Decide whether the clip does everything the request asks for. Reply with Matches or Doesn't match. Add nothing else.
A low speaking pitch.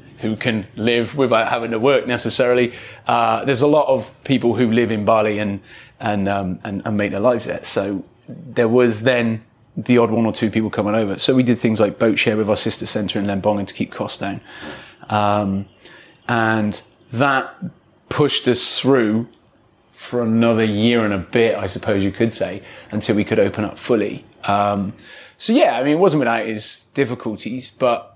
Matches